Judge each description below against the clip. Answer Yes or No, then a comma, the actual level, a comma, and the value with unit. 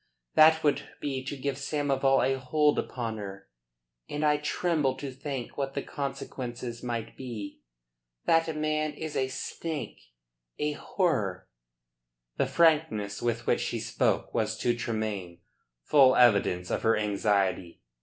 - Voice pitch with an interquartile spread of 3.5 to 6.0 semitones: Yes, average, 5.1 semitones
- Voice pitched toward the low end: Yes, low, 130 Hz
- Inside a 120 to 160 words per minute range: Yes, slow, 135 wpm